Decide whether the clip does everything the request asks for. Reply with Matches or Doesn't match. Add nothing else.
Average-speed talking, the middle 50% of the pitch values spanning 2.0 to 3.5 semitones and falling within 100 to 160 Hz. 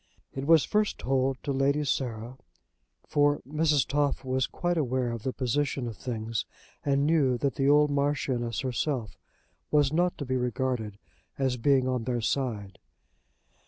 Matches